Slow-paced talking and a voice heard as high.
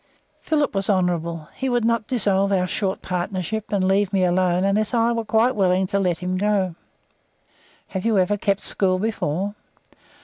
No: average, 170 wpm; high, 195 Hz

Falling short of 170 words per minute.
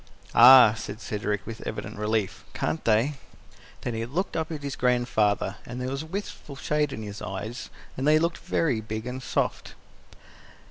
No: average, 175 wpm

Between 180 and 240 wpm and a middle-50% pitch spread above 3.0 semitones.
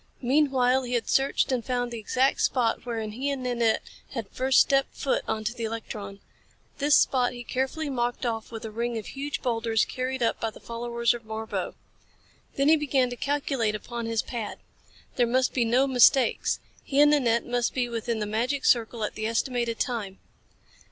No: average, 185 wpm; narrow, 2.5 semitones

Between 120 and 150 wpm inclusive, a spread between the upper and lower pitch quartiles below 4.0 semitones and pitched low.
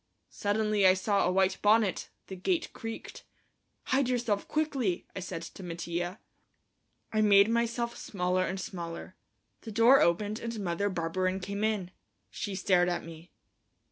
No: average, 145 wpm; average, 3.5 semitones; high, 200 Hz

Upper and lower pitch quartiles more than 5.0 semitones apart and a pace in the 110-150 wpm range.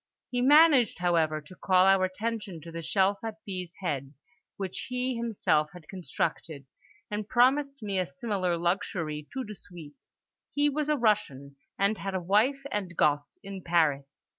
No: wide, 5.5 semitones; average, 165 wpm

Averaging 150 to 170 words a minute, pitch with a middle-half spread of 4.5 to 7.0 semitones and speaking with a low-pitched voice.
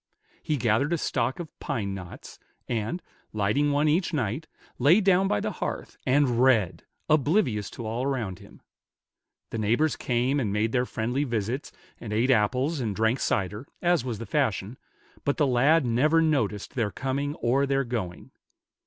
Yes: average, 165 wpm; average, 4.9 semitones; low, 125 Hz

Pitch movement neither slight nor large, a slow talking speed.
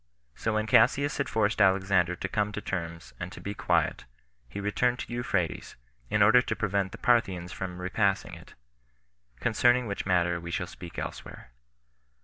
No: average, 3.5 semitones; average, 165 wpm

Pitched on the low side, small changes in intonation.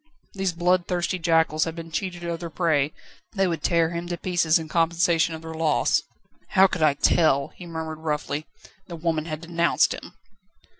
No: medium, 165 Hz; narrow, 1.5 semitones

